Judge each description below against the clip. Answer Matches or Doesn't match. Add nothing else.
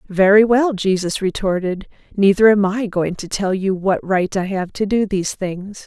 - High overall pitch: Matches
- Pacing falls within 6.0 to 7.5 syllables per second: Doesn't match